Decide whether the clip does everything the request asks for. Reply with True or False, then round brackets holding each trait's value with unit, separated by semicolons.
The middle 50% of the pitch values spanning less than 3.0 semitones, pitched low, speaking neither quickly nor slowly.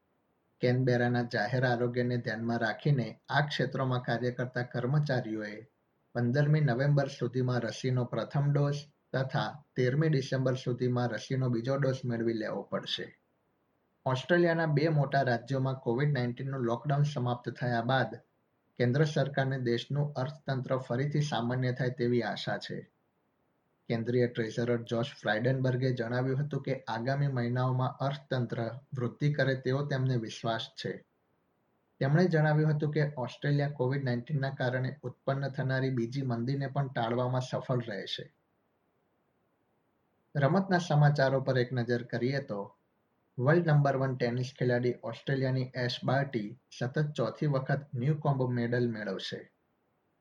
True (2.5 semitones; 130 Hz; 120 wpm)